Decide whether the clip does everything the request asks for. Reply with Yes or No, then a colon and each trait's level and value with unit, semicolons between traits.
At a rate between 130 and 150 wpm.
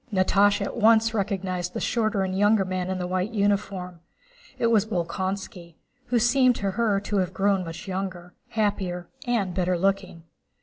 No: average, 165 wpm